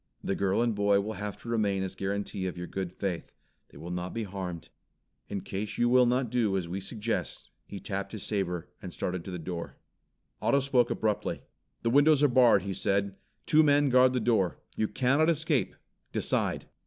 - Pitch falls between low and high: No, low, 100 Hz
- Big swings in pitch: No, average, 4.4 semitones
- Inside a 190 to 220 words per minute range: Yes, average, 200 wpm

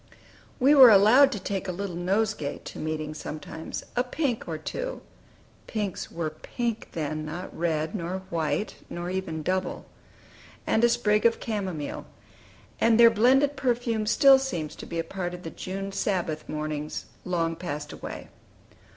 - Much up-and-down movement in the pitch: Yes, wide, 6.0 semitones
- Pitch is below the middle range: No, high, 190 Hz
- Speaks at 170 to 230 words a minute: No, average, 155 wpm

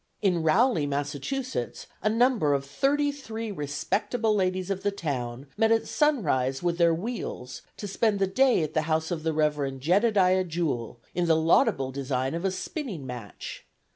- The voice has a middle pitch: Yes, medium, 170 Hz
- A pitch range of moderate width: No, wide, 7.2 semitones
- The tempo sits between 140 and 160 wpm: No, average, 170 wpm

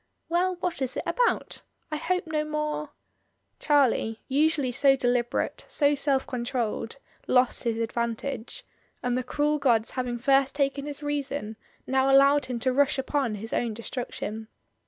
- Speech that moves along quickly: No, average, 155 wpm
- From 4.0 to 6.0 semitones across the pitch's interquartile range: No, average, 3.3 semitones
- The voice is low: No, very high, 270 Hz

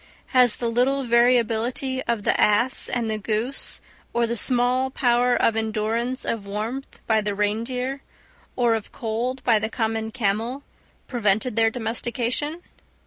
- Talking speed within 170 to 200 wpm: No, average, 140 wpm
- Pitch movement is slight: Yes, narrow, 2.3 semitones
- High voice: Yes, high, 235 Hz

